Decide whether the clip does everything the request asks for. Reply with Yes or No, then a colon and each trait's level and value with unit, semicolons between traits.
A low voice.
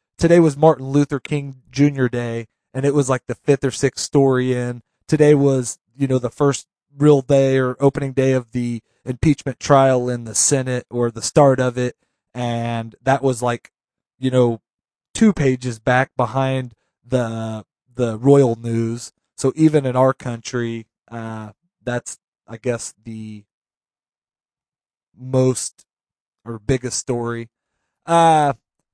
Yes: low, 125 Hz